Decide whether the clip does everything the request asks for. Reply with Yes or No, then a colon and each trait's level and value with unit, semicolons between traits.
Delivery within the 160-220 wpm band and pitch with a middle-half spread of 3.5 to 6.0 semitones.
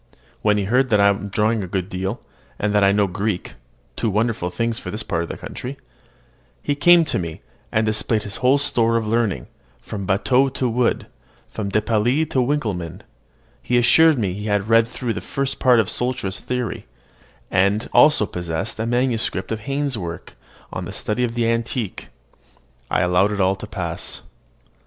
Yes: average, 190 wpm; average, 3.8 semitones